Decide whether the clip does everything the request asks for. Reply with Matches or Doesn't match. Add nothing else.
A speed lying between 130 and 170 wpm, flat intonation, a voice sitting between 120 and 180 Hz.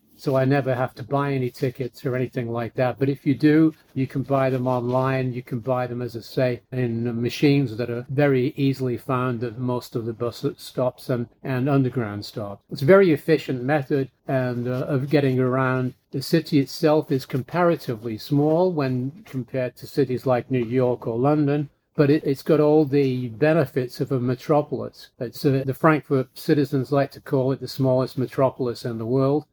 Doesn't match